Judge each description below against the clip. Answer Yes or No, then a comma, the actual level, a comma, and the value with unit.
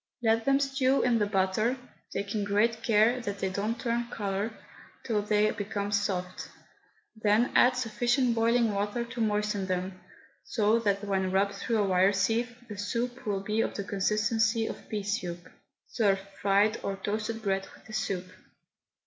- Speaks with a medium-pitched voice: No, high, 210 Hz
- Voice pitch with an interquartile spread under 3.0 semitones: Yes, narrow, 2.6 semitones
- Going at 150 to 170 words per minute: Yes, average, 165 wpm